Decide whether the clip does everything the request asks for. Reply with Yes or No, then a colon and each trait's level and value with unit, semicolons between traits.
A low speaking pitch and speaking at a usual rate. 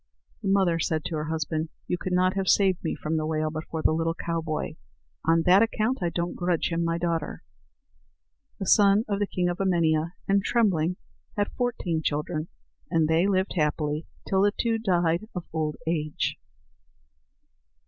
No: medium, 170 Hz; average, 175 wpm